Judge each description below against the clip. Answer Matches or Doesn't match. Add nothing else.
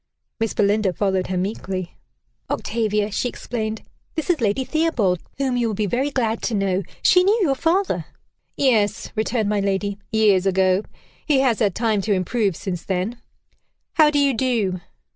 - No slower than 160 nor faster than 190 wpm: Matches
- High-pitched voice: Matches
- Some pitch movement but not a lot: Matches